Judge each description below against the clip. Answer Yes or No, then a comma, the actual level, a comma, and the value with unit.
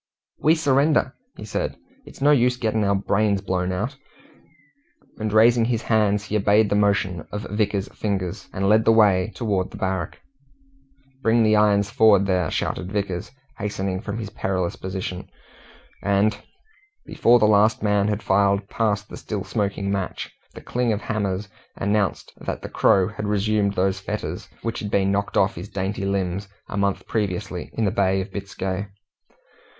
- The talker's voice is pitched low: Yes, low, 100 Hz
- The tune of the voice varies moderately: No, narrow, 1.9 semitones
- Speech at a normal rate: Yes, average, 165 wpm